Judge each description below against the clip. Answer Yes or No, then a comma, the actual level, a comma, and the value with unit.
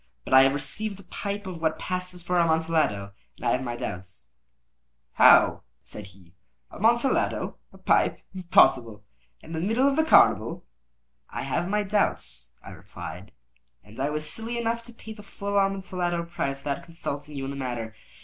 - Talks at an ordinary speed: Yes, average, 175 wpm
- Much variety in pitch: Yes, wide, 7.4 semitones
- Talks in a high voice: No, medium, 165 Hz